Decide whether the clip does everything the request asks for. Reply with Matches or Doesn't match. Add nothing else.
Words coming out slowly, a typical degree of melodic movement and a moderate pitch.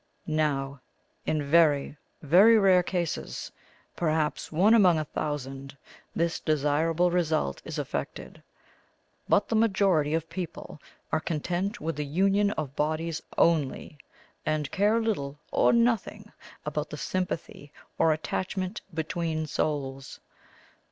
Matches